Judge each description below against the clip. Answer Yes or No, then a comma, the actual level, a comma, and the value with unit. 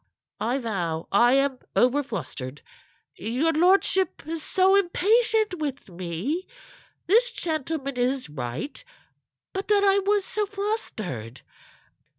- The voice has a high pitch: Yes, very high, 295 Hz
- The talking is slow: Yes, slow, 115 wpm